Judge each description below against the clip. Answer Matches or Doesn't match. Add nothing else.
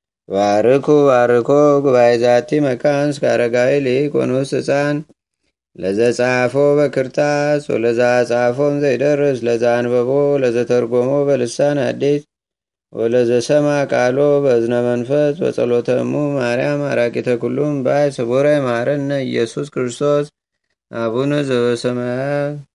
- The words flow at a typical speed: Matches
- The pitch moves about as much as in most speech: Matches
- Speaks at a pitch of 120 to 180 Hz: Matches